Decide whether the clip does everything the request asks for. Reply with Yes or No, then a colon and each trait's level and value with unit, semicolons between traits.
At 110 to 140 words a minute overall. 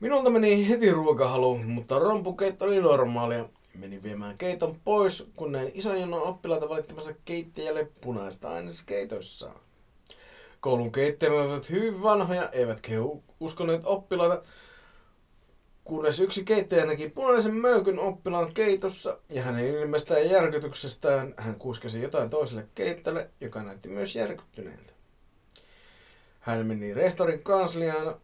Yes: average, 120 wpm